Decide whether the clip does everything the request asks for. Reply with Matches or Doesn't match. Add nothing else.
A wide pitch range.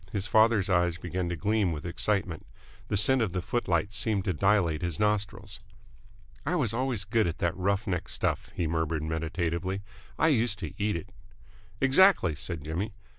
Doesn't match